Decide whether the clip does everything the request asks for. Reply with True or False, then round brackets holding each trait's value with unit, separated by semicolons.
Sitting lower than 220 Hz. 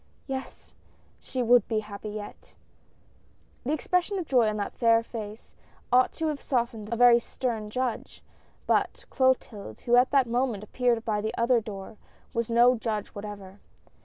False (235 Hz)